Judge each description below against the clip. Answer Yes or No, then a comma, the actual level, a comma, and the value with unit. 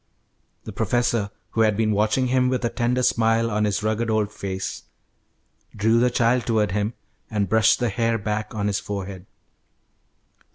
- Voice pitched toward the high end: No, low, 110 Hz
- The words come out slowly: No, average, 165 wpm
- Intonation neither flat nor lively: No, narrow, 2.1 semitones